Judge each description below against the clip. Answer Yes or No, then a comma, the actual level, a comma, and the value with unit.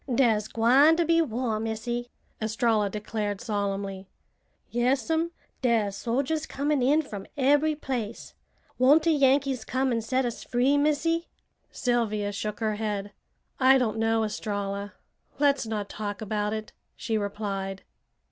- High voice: Yes, high, 230 Hz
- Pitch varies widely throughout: No, average, 4.4 semitones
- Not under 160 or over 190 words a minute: No, slow, 135 wpm